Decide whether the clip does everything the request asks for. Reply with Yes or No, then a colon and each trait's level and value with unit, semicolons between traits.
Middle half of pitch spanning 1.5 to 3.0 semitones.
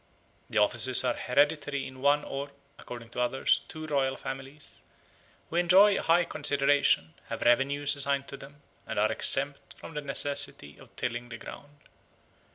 Yes: narrow, 2.6 semitones